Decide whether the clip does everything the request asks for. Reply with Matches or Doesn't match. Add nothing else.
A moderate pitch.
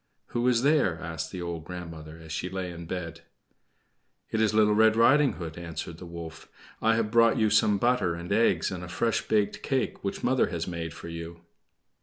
Doesn't match